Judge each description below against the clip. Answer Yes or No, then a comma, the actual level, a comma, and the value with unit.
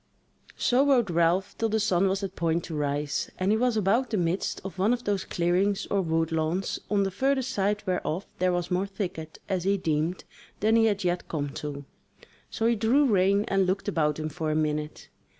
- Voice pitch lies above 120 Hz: Yes, high, 190 Hz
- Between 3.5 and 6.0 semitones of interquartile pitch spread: Yes, average, 4.1 semitones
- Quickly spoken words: Yes, fast, 210 wpm